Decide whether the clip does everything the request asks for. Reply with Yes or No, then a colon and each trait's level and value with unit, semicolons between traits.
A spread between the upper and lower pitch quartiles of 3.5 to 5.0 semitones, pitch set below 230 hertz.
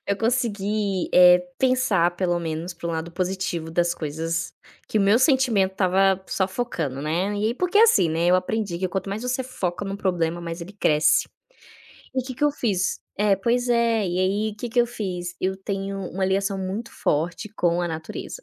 Yes: average, 3.9 semitones; high, 190 Hz